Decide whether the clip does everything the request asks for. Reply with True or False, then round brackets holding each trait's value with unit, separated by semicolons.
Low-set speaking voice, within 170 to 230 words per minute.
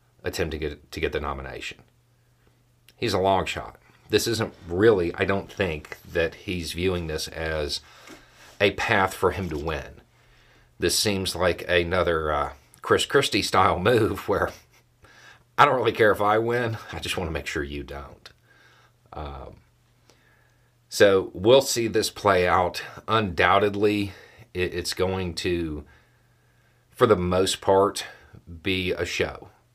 False (95 Hz; 145 wpm)